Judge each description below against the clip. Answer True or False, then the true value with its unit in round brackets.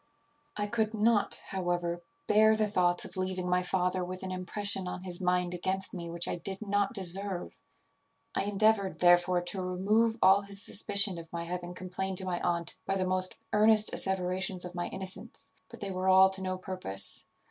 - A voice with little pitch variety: True (1.9 semitones)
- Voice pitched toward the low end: False (185 Hz)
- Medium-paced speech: True (185 wpm)